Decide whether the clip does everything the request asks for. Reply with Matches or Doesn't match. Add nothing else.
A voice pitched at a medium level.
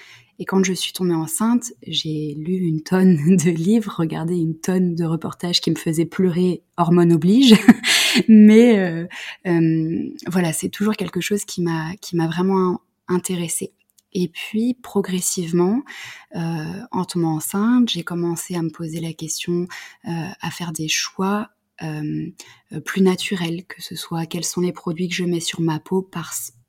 Matches